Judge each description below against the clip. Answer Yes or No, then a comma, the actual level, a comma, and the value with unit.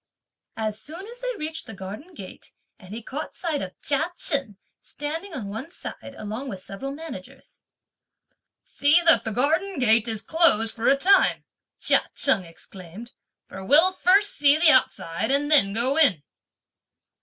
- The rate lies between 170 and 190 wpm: No, average, 160 wpm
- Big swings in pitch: Yes, wide, 6.9 semitones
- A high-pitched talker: Yes, very high, 275 Hz